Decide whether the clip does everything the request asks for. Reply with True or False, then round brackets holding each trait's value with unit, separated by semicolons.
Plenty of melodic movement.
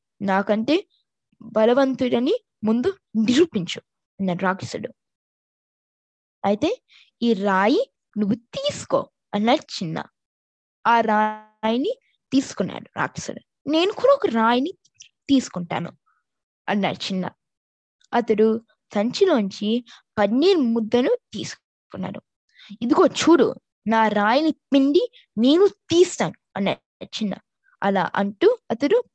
True (6.9 semitones)